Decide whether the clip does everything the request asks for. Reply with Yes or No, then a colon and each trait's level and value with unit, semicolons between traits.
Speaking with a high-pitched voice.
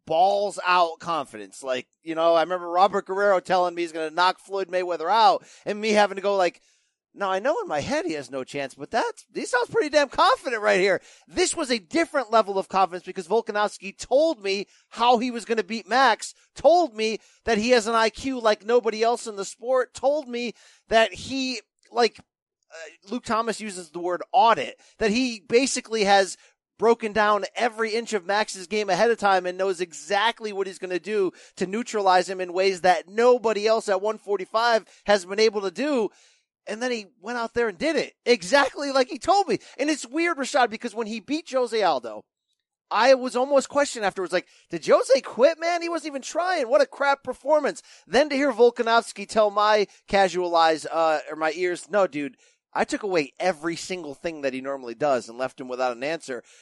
Yes: high, 215 Hz